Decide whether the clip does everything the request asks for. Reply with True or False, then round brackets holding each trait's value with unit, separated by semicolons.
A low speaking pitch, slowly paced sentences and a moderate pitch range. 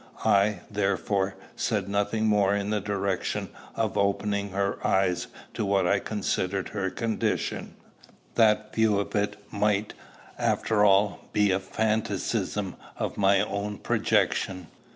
False (100 Hz; 130 wpm; 1.2 semitones)